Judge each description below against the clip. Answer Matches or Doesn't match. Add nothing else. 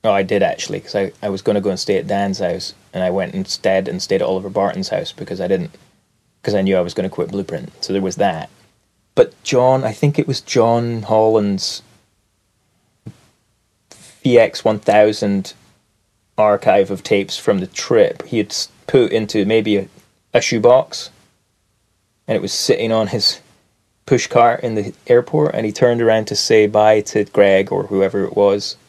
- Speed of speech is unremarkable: Matches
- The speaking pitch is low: Matches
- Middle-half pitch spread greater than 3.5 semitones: Doesn't match